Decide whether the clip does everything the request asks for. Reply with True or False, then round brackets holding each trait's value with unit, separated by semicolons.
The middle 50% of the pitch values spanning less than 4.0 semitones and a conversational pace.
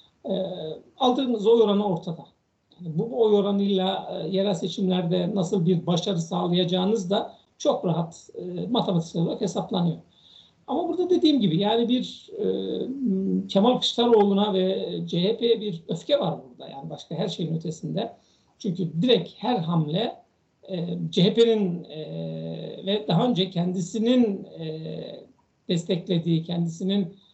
False (4.3 semitones; 125 wpm)